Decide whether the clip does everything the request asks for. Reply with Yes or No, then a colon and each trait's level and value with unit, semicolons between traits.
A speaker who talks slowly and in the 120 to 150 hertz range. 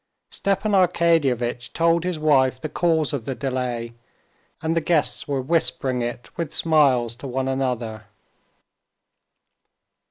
Yes: slow, 125 wpm; medium, 140 Hz